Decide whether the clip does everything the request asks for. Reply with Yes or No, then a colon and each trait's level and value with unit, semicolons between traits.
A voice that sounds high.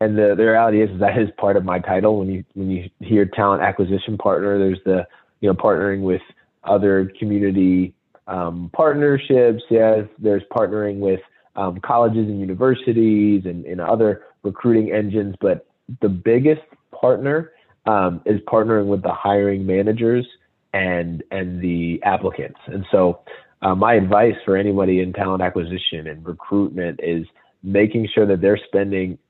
No: low, 100 Hz